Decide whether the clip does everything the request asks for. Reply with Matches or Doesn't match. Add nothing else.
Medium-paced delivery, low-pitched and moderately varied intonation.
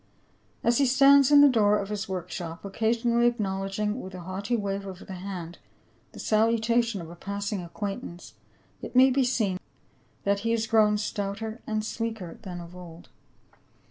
Doesn't match